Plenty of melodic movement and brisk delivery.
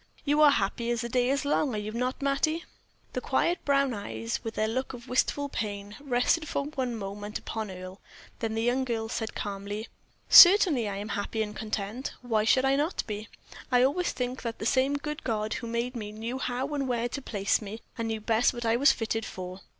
No: average, 3.9 semitones; fast, 215 wpm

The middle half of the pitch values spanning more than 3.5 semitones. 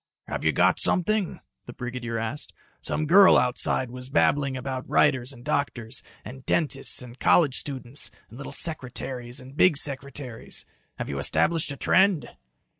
No: average, 3.0 semitones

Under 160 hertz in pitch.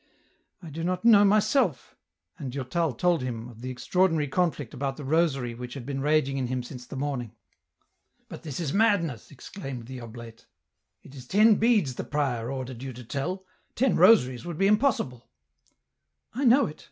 Yes: medium, 140 Hz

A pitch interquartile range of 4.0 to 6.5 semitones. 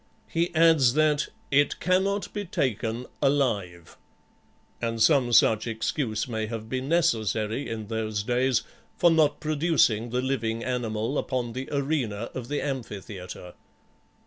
Yes: average, 4.7 semitones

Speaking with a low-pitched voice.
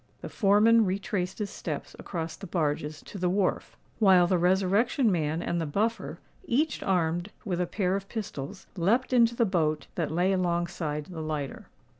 No: medium, 180 Hz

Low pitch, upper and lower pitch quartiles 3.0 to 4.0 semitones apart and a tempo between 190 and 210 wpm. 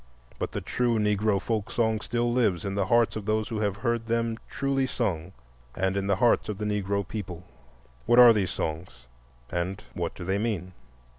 Yes: low, 105 Hz; average, 3.3 semitones; average, 195 wpm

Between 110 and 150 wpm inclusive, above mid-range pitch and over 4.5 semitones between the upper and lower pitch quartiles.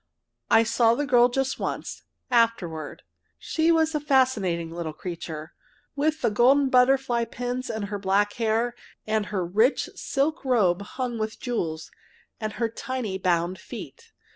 Yes: average, 145 wpm; high, 230 Hz; average, 5.2 semitones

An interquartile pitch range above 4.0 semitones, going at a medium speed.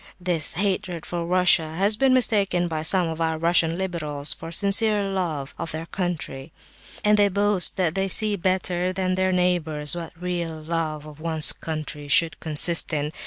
No: average, 3.0 semitones; average, 170 wpm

